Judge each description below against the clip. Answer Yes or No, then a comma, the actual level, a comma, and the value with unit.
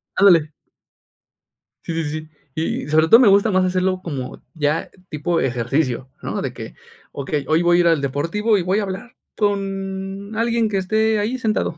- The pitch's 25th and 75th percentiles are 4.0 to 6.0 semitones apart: Yes, average, 4.6 semitones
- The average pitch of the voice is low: No, medium, 185 Hz